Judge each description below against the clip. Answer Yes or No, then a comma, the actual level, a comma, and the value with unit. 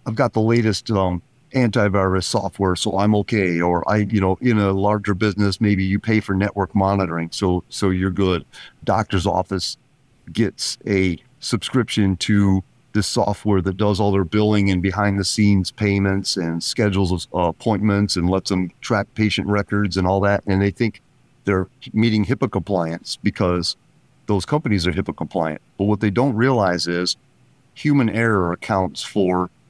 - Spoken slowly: No, average, 170 wpm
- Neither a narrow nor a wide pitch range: No, narrow, 2.2 semitones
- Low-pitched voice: Yes, low, 100 Hz